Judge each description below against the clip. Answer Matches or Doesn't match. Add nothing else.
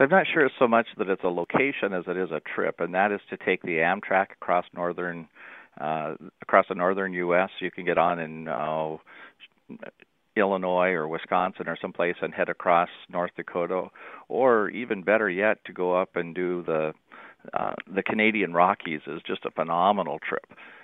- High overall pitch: Doesn't match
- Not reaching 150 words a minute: Doesn't match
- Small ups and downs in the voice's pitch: Matches